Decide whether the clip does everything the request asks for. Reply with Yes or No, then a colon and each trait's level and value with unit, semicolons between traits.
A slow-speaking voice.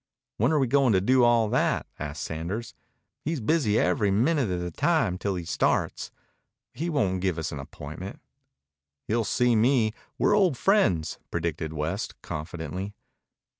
No: average, 155 wpm